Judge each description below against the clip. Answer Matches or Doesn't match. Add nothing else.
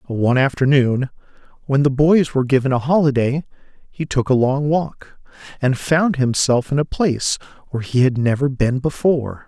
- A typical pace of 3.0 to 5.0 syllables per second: Doesn't match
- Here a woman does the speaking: Doesn't match